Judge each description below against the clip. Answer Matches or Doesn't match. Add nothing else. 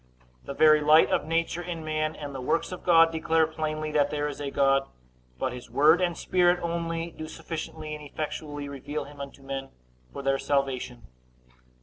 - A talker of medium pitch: Matches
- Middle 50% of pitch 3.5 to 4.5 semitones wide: Doesn't match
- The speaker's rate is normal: Matches